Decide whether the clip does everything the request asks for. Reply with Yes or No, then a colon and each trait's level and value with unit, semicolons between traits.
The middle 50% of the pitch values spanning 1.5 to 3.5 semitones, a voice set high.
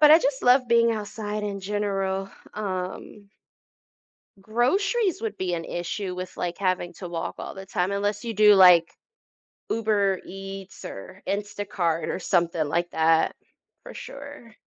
Yes: average, 3.2 semitones; high, 200 Hz